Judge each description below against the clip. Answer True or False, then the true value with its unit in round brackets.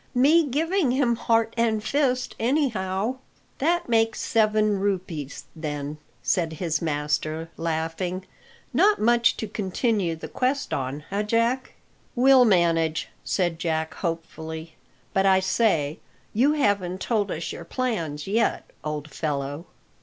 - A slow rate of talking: True (125 wpm)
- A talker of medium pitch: False (195 Hz)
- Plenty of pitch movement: True (6.6 semitones)